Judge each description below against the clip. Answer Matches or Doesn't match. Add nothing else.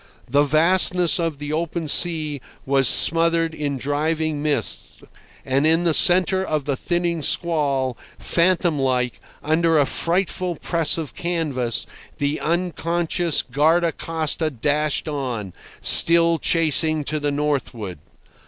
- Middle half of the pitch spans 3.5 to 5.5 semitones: Doesn't match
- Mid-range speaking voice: Matches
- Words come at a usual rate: Doesn't match